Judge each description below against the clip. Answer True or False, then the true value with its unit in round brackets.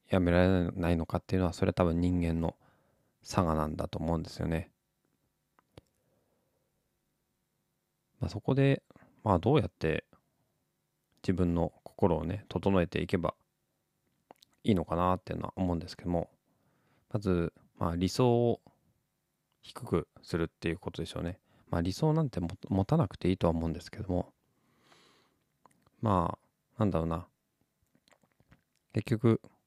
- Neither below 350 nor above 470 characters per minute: False (275 characters per minute)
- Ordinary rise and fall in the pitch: True (4.9 semitones)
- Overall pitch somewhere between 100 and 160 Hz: False (90 Hz)